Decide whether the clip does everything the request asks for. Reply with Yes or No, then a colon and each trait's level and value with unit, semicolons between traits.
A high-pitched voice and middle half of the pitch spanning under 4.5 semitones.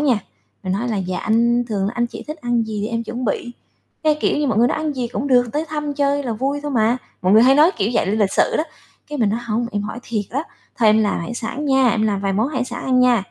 Yes: high, 240 Hz; average, 3.8 semitones